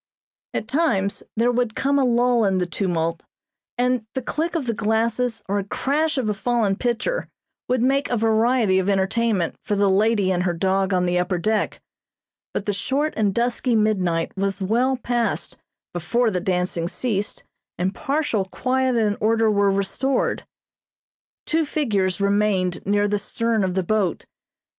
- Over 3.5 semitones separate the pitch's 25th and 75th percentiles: Yes, average, 4.3 semitones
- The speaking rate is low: No, average, 160 wpm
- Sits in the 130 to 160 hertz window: No, high, 215 Hz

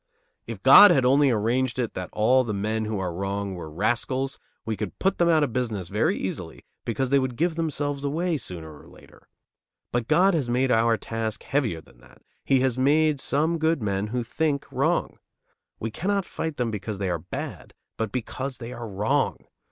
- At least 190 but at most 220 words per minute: Yes, average, 195 wpm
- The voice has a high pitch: No, low, 125 Hz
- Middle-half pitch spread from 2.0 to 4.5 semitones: No, average, 5.1 semitones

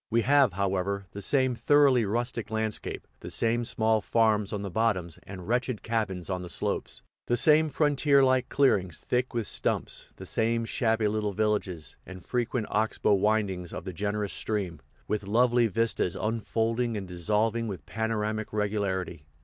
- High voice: No, low, 110 Hz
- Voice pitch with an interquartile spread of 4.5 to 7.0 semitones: No, average, 2.9 semitones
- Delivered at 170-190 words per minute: No, average, 160 wpm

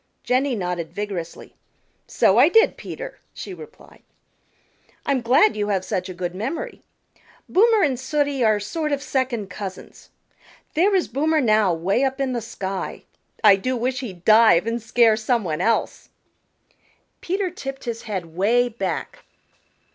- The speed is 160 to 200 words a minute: No, average, 150 wpm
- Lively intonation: Yes, wide, 5.7 semitones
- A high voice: Yes, high, 235 Hz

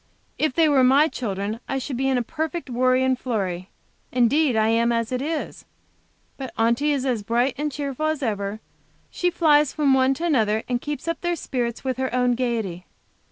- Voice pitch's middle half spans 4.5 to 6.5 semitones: No, average, 4.0 semitones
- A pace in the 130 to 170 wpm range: No, average, 200 wpm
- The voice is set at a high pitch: Yes, very high, 255 Hz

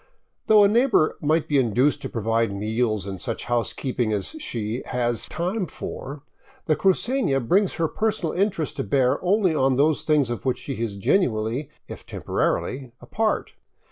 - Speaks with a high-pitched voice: No, low, 135 Hz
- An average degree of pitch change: No, wide, 7.6 semitones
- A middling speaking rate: Yes, average, 170 wpm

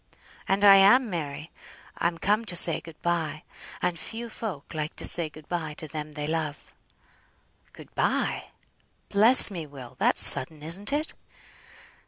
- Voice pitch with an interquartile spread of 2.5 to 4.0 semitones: No, average, 4.6 semitones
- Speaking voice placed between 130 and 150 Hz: No, medium, 165 Hz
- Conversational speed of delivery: Yes, average, 155 wpm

